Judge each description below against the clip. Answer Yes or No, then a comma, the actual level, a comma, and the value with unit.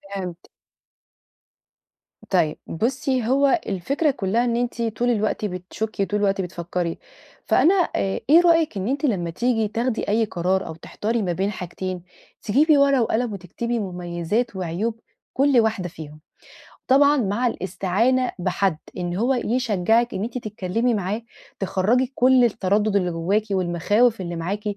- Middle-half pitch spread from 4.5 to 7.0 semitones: Yes, average, 4.9 semitones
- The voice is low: No, high, 210 Hz